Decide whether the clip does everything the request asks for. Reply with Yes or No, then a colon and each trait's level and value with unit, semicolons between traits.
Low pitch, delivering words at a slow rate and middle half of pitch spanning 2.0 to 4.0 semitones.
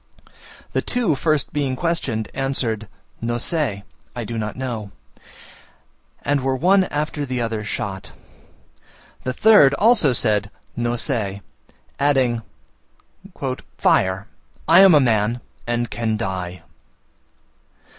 No: low, 120 Hz; slow, 115 wpm; average, 4.9 semitones